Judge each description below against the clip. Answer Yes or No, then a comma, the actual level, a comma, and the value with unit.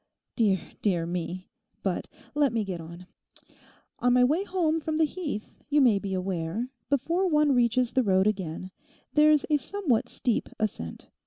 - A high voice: Yes, high, 240 Hz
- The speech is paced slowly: No, average, 160 wpm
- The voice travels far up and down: Yes, wide, 8.0 semitones